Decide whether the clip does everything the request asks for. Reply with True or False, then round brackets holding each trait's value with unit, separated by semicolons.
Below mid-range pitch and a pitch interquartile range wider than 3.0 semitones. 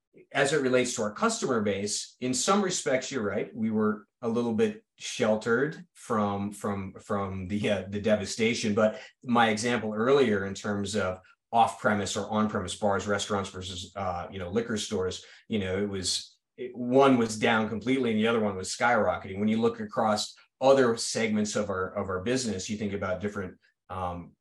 True (105 Hz; 3.5 semitones)